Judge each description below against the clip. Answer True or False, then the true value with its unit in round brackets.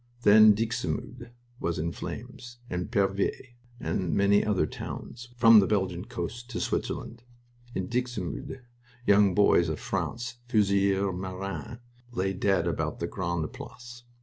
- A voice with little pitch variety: False (4.2 semitones)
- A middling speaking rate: False (130 wpm)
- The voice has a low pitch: True (100 Hz)